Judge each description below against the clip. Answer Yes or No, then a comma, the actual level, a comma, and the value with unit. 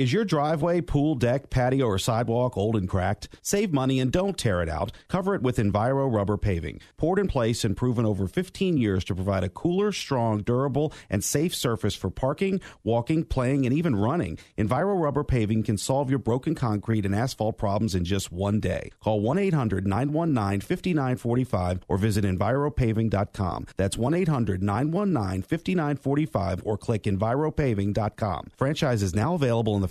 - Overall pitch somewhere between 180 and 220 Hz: No, low, 120 Hz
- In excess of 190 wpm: No, average, 170 wpm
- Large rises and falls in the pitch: Yes, wide, 6.2 semitones